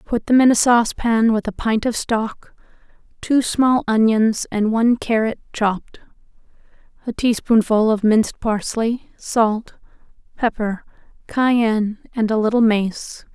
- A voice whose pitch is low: No, high, 225 Hz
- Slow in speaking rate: Yes, slow, 130 wpm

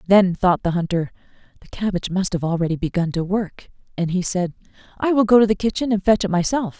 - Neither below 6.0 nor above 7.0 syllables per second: Yes, 6.1 syllables/s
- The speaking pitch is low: No, high, 190 Hz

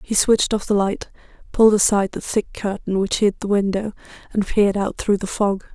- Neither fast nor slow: No, fast, 210 wpm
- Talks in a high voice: Yes, high, 205 Hz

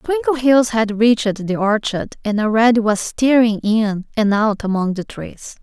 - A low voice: No, high, 220 Hz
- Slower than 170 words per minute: Yes, average, 160 wpm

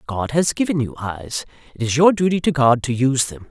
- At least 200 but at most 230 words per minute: No, fast, 240 wpm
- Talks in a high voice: No, low, 135 Hz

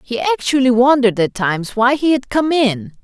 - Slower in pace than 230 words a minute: Yes, average, 200 wpm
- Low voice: No, high, 245 Hz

